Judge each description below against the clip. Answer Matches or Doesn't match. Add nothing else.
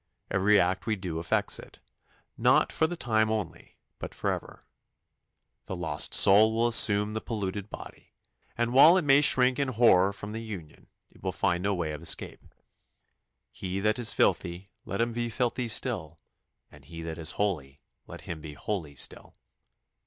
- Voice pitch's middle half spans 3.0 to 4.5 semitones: Doesn't match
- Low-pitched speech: Matches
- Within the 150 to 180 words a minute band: Matches